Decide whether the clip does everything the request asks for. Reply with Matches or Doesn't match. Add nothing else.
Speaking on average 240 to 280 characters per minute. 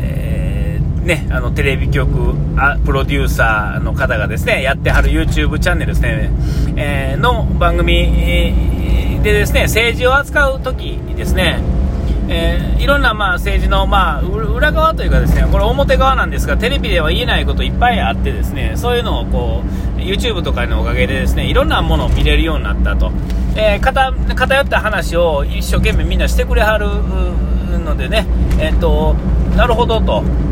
Doesn't match